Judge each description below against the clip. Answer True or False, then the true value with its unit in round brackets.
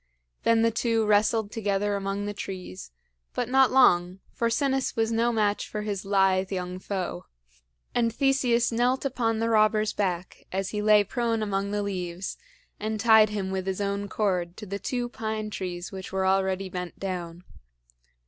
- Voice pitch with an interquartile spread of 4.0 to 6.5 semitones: False (3.0 semitones)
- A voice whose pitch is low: False (205 Hz)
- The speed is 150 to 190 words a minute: True (170 wpm)